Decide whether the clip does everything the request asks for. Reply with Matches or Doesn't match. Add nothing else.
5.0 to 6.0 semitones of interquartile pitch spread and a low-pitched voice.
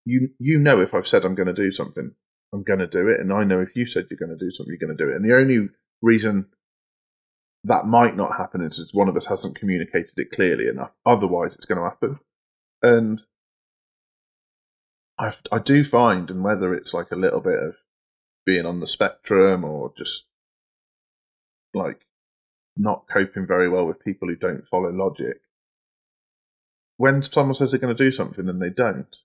Matches